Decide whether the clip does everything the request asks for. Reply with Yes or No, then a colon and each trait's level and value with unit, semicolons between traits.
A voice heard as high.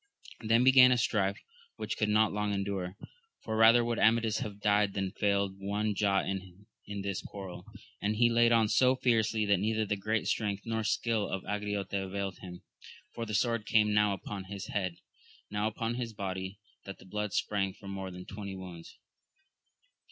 No: low, 105 Hz